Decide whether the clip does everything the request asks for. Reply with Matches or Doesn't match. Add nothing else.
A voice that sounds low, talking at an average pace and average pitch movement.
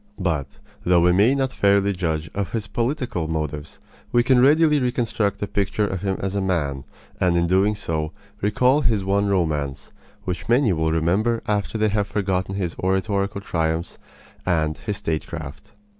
Matches